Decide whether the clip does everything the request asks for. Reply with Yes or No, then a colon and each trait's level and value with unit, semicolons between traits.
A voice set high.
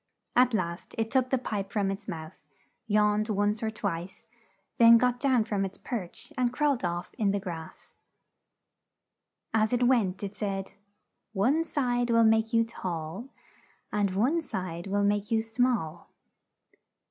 Yes: high, 215 Hz